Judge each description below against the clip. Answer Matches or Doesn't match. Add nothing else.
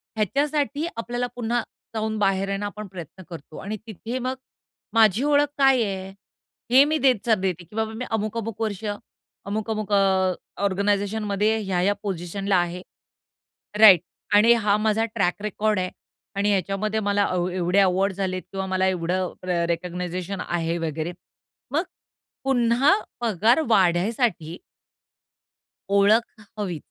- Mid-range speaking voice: Doesn't match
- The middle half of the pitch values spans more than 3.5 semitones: Doesn't match